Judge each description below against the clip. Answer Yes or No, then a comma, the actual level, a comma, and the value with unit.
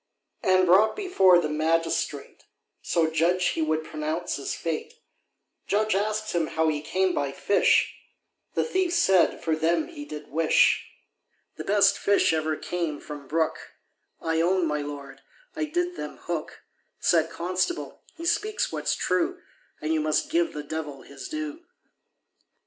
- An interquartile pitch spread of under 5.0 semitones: No, wide, 5.6 semitones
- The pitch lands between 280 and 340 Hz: No, medium, 170 Hz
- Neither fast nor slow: Yes, average, 150 wpm